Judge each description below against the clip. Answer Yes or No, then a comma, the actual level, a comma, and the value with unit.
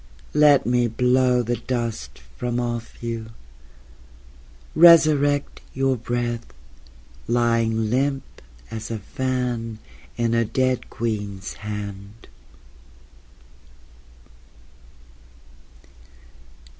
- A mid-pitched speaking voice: No, low, 120 Hz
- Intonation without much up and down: Yes, narrow, 2.3 semitones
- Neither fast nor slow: No, slow, 75 wpm